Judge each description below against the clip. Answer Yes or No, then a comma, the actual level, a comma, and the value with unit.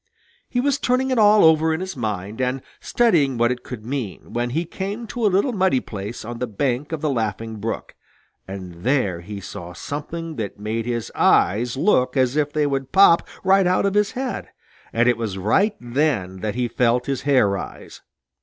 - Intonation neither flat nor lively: No, wide, 7.3 semitones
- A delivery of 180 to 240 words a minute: Yes, average, 200 wpm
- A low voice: Yes, low, 130 Hz